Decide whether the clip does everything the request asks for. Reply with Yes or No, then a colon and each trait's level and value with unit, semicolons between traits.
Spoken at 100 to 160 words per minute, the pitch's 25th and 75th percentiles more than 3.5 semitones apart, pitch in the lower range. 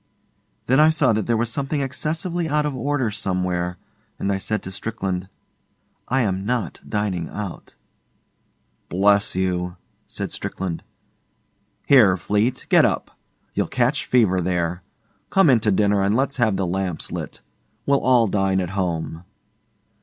Yes: average, 150 wpm; wide, 5.5 semitones; low, 105 Hz